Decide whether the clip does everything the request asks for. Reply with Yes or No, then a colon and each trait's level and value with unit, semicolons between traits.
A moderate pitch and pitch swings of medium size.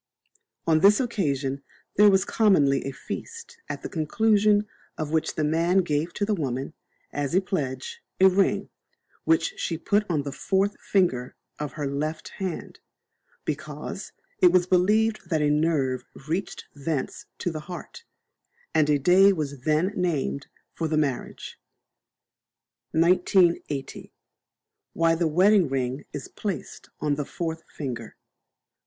Yes: medium, 165 Hz; average, 4.8 semitones